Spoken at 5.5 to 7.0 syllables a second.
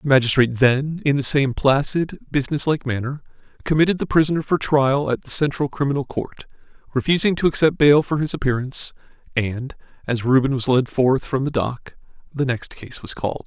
Yes: 5.6 syllables/s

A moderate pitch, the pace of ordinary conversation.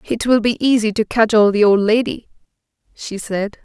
No: high, 220 Hz; average, 180 wpm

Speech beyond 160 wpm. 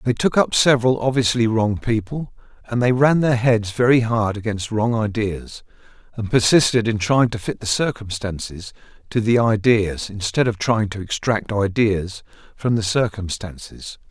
No: average, 155 wpm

